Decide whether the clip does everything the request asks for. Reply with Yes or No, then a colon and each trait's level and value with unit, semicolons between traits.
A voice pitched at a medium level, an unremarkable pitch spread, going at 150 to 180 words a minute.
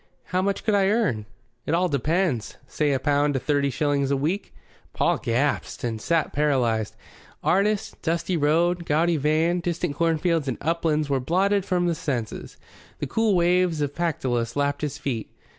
Yes: medium, 155 Hz; average, 3.8 semitones; average, 165 wpm